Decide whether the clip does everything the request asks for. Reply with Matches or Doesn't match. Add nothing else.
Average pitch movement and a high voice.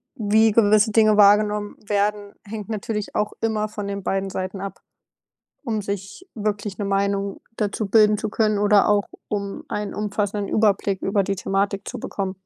Doesn't match